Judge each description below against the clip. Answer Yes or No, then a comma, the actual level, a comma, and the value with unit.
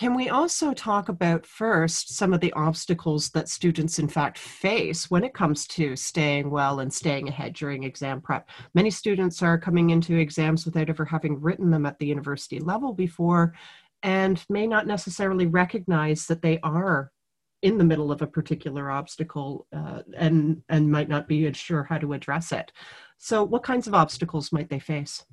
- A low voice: No, medium, 160 Hz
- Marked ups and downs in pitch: No, average, 3.3 semitones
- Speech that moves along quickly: No, average, 180 wpm